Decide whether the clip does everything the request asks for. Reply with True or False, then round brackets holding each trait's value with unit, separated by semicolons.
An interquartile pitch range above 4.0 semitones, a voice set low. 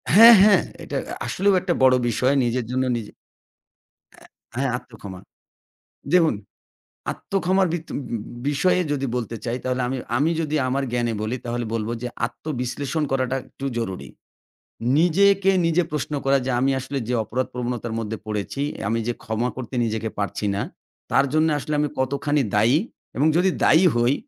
True (4.6 semitones; 130 Hz)